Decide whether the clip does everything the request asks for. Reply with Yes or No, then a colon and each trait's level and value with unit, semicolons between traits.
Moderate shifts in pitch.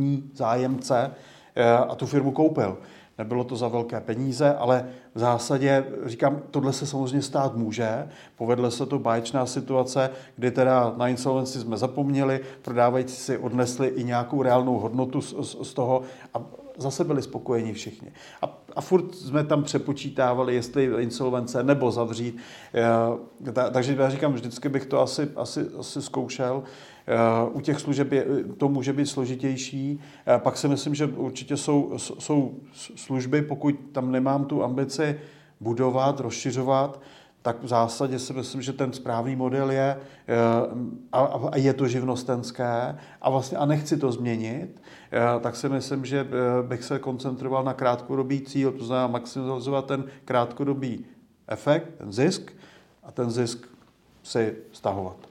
No: narrow, 2.0 semitones